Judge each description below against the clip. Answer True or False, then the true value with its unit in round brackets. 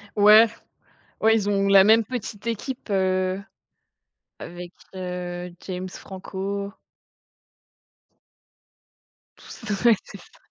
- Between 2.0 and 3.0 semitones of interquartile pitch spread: True (2.4 semitones)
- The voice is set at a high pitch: True (195 Hz)